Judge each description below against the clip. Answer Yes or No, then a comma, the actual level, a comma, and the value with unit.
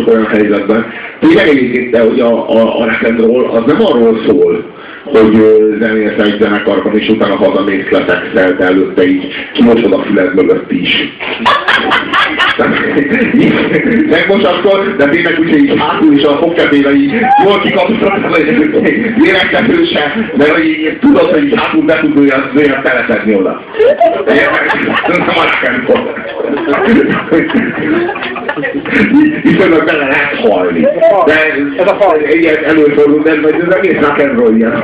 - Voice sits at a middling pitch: Yes, medium, 150 Hz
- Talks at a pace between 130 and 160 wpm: Yes, average, 150 wpm